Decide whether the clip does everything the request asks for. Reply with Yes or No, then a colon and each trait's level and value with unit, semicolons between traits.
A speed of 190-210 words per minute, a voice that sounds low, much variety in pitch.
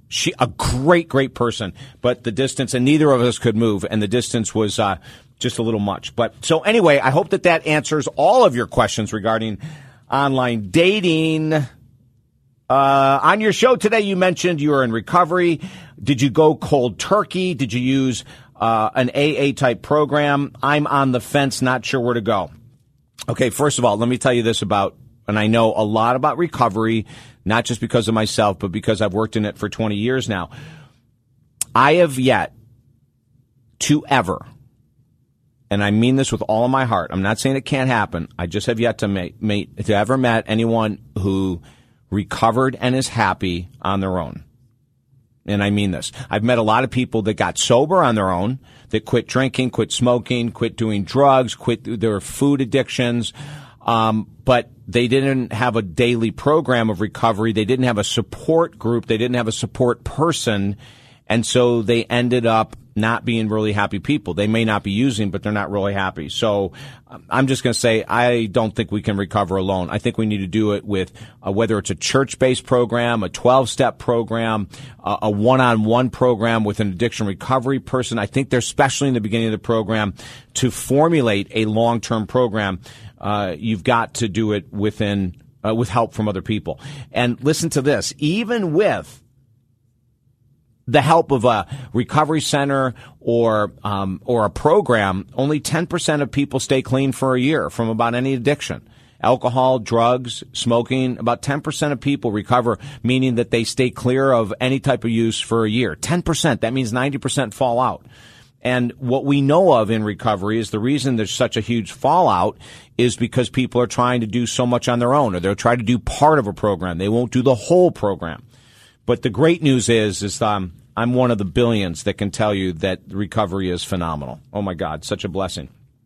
No: average, 195 wpm; low, 120 Hz; average, 3.4 semitones